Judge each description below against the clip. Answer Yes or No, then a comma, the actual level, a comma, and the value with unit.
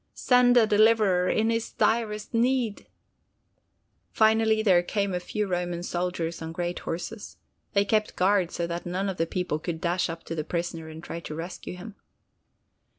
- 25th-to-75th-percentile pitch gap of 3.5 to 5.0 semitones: Yes, average, 4.1 semitones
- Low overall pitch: No, medium, 180 Hz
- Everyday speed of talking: Yes, average, 170 wpm